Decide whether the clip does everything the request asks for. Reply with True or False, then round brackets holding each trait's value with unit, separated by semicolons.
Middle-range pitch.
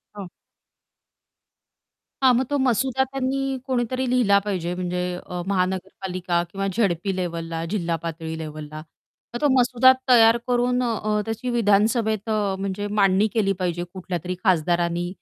False (200 Hz)